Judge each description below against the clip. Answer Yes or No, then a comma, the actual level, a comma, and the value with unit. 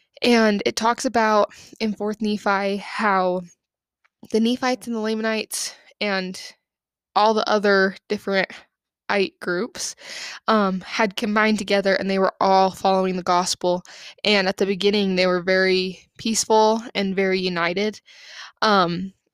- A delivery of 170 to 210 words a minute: No, slow, 135 wpm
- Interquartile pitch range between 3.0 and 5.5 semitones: No, narrow, 2.5 semitones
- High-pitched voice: Yes, high, 200 Hz